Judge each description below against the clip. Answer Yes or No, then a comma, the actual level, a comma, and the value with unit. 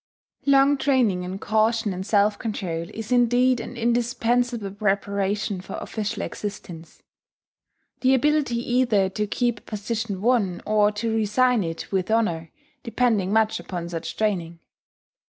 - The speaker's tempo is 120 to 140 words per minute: Yes, slow, 135 wpm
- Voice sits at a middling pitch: No, high, 215 Hz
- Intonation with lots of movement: No, average, 3.8 semitones